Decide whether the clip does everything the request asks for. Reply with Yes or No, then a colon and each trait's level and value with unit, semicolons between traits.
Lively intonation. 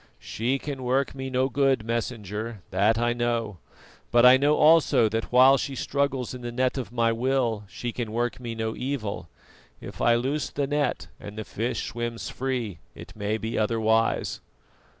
No: average, 2.8 semitones